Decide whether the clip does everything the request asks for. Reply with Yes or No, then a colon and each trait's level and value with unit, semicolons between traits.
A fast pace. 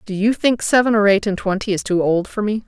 Yes: fast, 290 wpm